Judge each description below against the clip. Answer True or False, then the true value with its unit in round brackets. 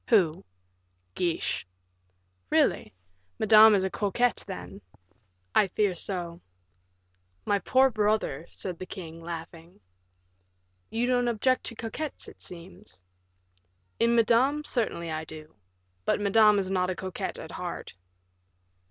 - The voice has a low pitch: False (200 Hz)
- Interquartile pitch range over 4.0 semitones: True (4.7 semitones)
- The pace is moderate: False (120 wpm)